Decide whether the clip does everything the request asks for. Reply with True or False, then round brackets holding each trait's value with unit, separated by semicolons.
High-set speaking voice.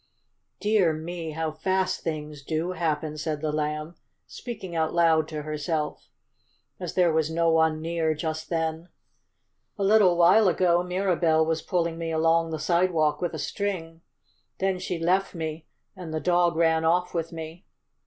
False (165 Hz)